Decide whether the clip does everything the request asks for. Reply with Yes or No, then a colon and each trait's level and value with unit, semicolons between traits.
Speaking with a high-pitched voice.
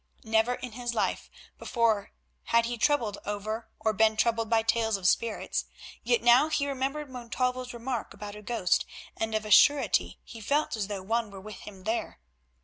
Yes: high, 230 Hz